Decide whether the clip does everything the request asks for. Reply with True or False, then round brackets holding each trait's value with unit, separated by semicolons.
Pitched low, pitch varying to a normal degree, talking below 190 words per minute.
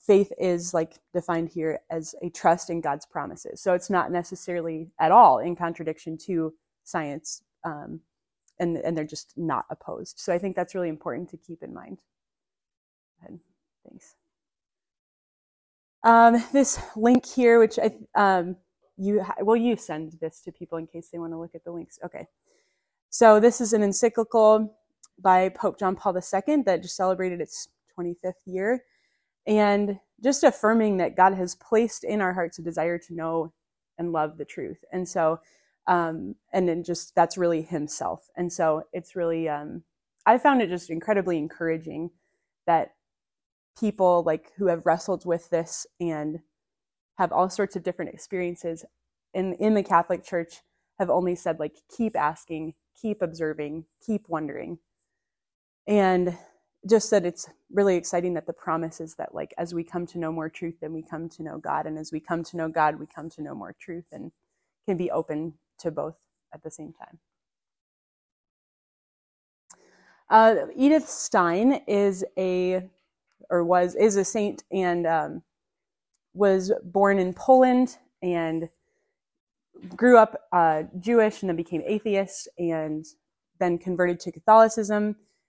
False (175 Hz; 3.8 semitones; 160 wpm)